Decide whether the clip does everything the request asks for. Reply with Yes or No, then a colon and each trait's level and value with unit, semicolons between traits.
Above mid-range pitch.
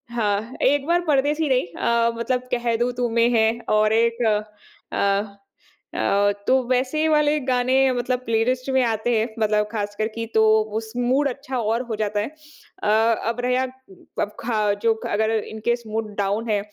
Yes: high, 235 Hz